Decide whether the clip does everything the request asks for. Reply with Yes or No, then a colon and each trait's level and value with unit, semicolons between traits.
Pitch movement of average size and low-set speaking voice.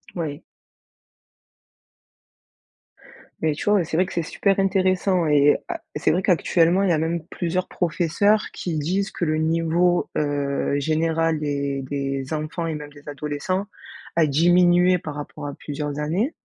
No: average, 3.3 semitones; medium, 160 Hz